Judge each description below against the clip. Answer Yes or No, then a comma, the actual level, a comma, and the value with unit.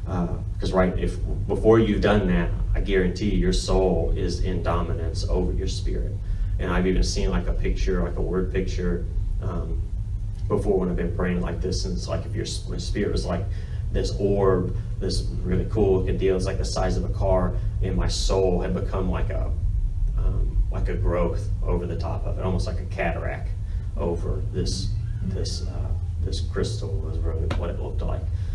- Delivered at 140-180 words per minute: No, average, 195 wpm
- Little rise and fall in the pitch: Yes, narrow, 1.5 semitones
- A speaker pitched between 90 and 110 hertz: Yes, very low, 95 Hz